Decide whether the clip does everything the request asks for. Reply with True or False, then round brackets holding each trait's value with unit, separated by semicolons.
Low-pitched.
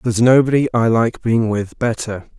True (115 Hz)